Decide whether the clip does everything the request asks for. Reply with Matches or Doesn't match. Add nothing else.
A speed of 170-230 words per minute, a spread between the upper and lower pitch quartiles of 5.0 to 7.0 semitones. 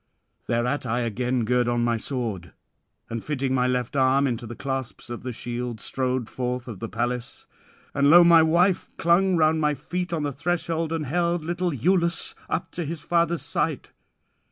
Matches